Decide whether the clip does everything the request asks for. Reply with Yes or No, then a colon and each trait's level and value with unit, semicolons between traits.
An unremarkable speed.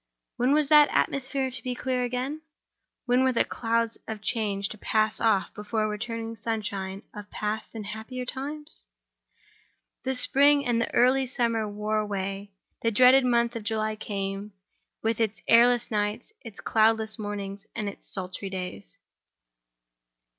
Yes: average, 150 wpm